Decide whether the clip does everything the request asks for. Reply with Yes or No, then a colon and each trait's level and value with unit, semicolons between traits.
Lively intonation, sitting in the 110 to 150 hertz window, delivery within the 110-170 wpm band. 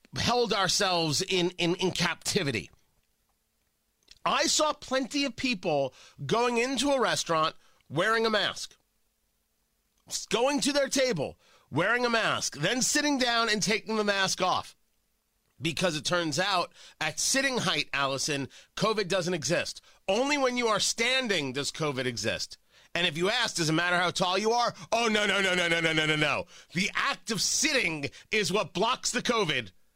No: wide, 6.0 semitones; high, 190 Hz; average, 165 wpm